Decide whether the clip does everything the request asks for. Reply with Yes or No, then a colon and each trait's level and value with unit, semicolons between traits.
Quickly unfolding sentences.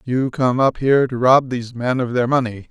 Yes: fast, 245 wpm